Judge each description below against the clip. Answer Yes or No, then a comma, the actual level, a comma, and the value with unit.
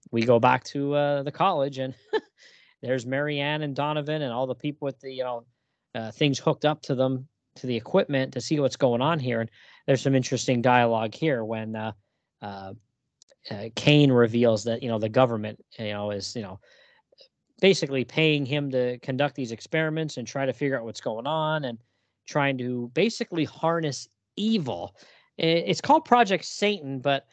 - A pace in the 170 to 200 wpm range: Yes, average, 180 wpm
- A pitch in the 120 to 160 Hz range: Yes, low, 135 Hz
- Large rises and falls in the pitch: No, average, 4.2 semitones